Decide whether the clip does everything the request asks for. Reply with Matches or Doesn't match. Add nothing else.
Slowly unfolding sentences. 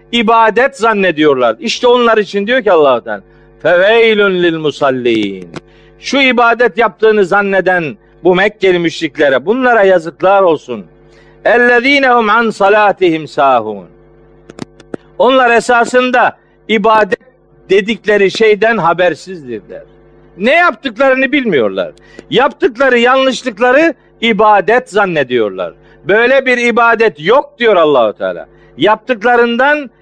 Matches